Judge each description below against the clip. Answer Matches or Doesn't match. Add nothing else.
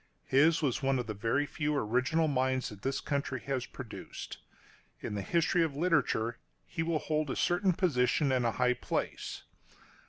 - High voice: Doesn't match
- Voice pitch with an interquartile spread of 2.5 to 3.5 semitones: Doesn't match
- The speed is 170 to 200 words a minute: Matches